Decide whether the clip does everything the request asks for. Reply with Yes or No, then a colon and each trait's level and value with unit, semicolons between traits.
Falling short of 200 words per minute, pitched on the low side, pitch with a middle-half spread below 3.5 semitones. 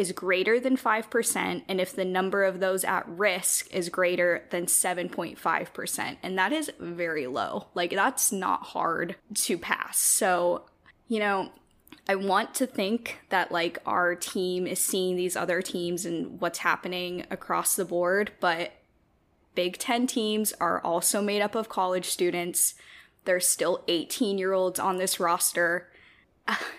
No: average, 155 wpm; medium, 185 Hz; narrow, 2.6 semitones